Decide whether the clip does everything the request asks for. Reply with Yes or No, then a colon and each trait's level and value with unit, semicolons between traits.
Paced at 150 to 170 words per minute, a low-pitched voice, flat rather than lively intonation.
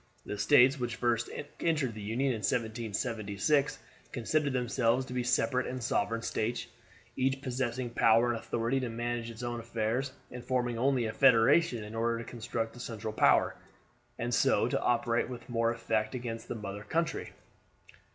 Yes: average, 165 wpm; low, 120 Hz; narrow, 2.0 semitones